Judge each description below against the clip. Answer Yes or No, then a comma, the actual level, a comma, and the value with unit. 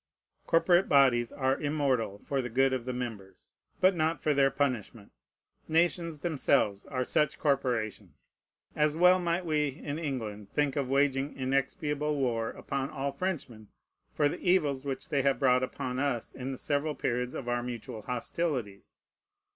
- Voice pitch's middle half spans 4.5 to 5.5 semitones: No, average, 3.4 semitones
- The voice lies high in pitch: No, low, 135 Hz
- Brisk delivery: No, average, 155 wpm